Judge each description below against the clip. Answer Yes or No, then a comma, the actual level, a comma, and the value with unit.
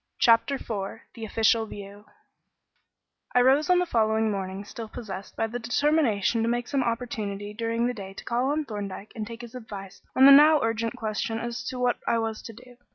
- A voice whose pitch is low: No, high, 230 Hz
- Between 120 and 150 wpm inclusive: No, average, 200 wpm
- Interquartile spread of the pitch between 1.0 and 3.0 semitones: Yes, average, 2.7 semitones